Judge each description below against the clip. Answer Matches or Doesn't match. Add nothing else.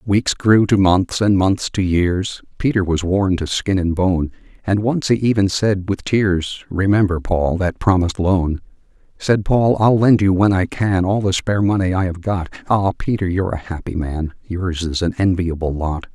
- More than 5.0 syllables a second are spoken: Doesn't match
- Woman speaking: Doesn't match